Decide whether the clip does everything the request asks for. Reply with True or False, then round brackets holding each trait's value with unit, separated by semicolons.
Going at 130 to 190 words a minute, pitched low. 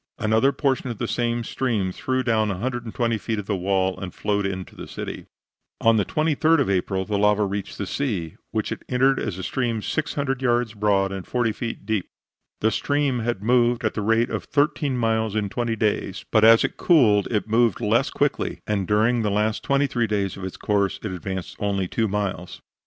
False (200 wpm; 110 Hz)